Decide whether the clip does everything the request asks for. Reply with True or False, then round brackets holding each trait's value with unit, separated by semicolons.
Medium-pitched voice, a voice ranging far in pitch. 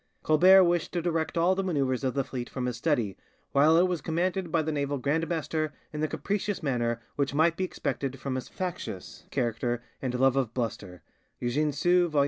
False (150 Hz; 4.8 semitones)